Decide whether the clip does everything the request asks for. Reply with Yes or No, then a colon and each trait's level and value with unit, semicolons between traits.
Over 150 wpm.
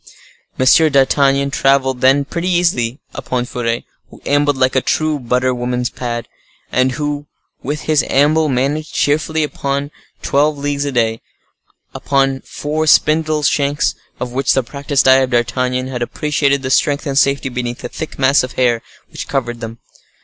Yes: average, 160 wpm